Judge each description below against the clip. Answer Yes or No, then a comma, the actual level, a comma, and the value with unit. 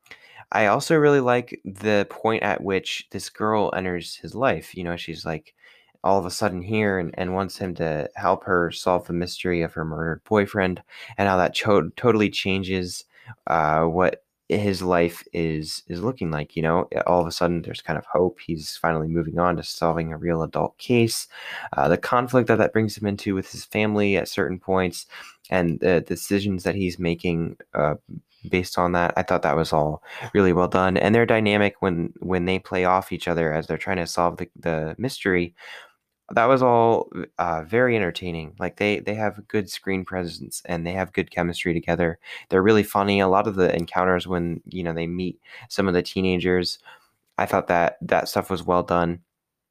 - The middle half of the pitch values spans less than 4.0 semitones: Yes, average, 2.9 semitones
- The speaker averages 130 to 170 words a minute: No, average, 200 wpm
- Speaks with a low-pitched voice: Yes, very low, 90 Hz